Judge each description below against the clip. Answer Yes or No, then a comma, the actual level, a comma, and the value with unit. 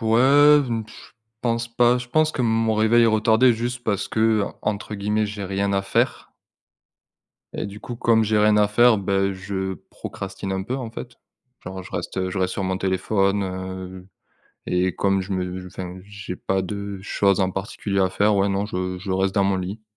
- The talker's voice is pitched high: No, low, 100 Hz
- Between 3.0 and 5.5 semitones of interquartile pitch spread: No, narrow, 2.6 semitones